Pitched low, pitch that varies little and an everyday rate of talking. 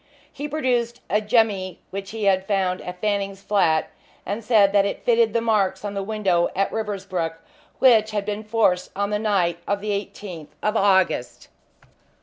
No: high, 200 Hz; narrow, 2.2 semitones; average, 170 wpm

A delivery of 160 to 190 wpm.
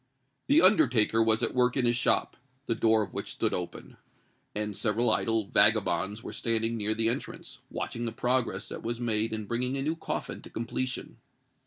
Yes: average, 185 wpm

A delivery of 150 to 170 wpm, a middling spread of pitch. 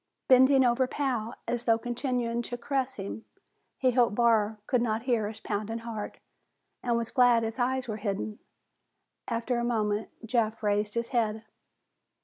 No: average, 155 wpm; narrow, 2.2 semitones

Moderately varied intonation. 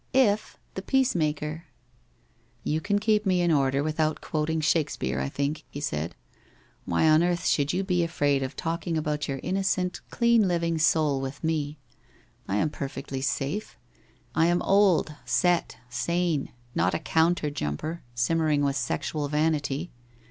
Yes: average, 3.6 semitones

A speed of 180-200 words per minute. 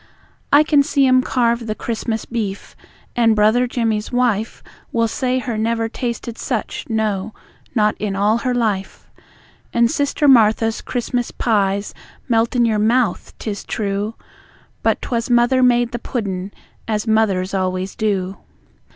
No: average, 140 wpm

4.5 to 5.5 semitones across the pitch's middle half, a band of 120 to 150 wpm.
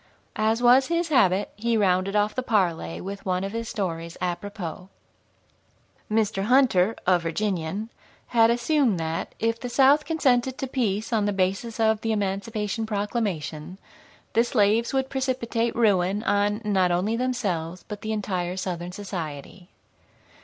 No: average, 4.1 semitones; average, 145 wpm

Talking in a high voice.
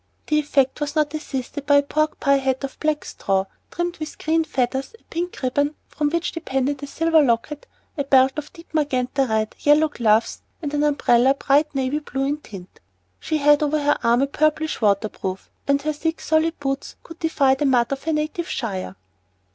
Yes: very high, 285 Hz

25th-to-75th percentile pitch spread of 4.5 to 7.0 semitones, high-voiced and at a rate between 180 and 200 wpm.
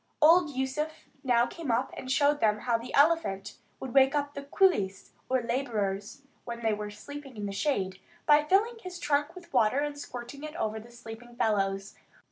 Yes: average, 5.2 semitones; very high, 260 Hz; average, 185 wpm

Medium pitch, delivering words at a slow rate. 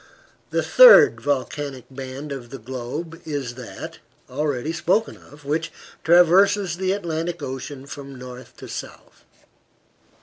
Yes: medium, 145 Hz; slow, 125 wpm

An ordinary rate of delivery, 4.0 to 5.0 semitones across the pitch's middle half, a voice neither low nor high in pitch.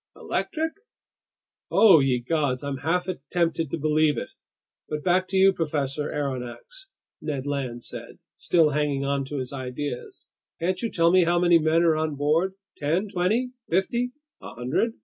Yes: average, 160 wpm; average, 4.4 semitones; medium, 155 Hz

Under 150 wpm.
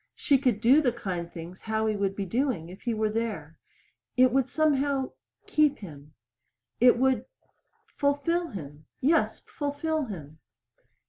Yes: average, 140 wpm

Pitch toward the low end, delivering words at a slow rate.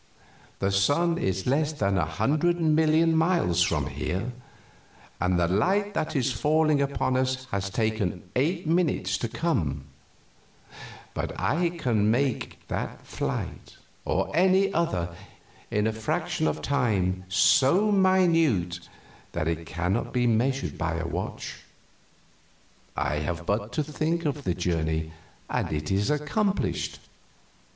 Yes: low, 125 Hz; slow, 130 wpm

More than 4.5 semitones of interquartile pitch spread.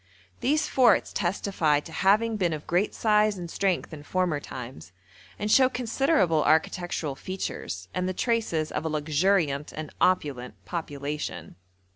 Yes: wide, 5.4 semitones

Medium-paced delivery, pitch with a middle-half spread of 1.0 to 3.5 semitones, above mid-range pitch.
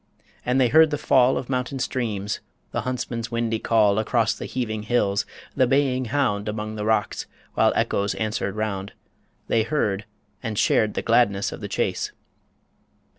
No: average, 160 wpm; average, 3.1 semitones; low, 115 Hz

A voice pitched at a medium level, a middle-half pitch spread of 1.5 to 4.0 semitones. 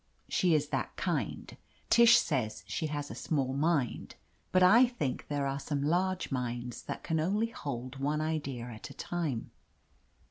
No: medium, 145 Hz; average, 4.8 semitones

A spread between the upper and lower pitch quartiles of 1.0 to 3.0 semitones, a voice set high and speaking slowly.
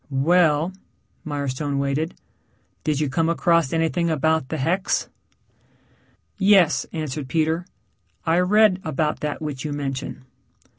No: average, 2.7 semitones; medium, 160 Hz; slow, 115 wpm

